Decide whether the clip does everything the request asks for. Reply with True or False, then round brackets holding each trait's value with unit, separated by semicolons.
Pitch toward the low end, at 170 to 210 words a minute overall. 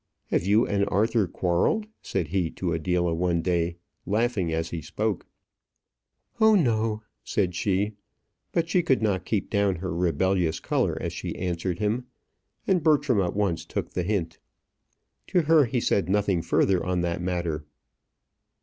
False (95 Hz; 155 wpm)